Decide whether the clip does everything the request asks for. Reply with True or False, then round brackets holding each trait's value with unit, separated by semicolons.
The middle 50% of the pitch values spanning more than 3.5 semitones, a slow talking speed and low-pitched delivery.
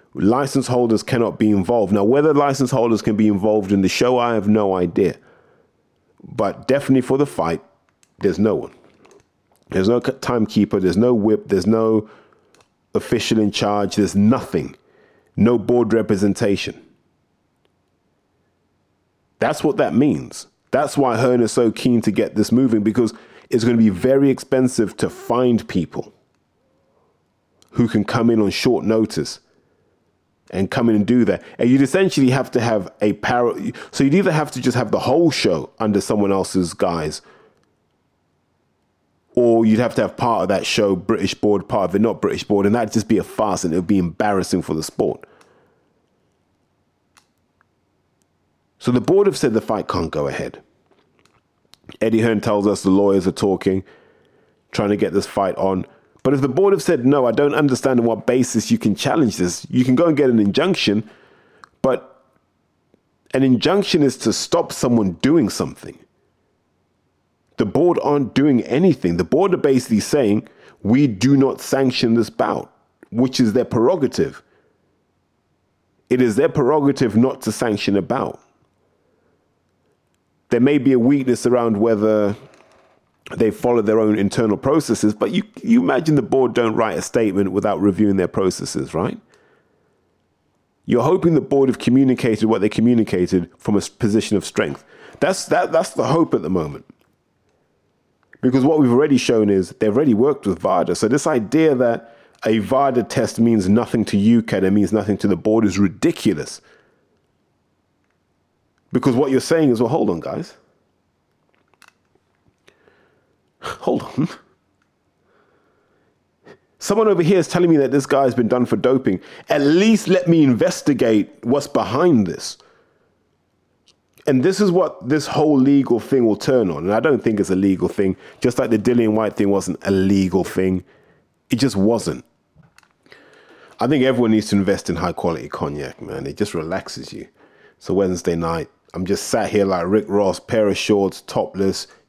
False (4.2 semitones; 165 wpm; 115 Hz)